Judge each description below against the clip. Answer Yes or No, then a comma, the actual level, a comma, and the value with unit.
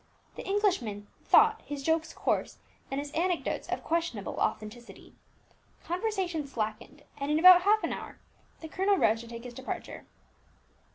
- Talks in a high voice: Yes, very high, 310 Hz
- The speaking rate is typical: Yes, average, 150 wpm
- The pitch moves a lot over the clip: Yes, wide, 7.6 semitones